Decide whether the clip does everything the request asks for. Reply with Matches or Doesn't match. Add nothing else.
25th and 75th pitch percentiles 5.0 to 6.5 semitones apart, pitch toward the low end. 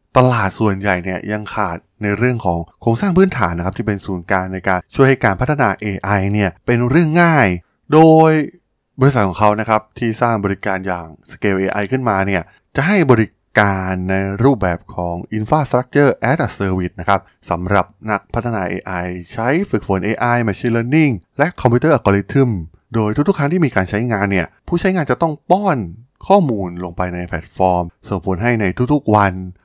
Matches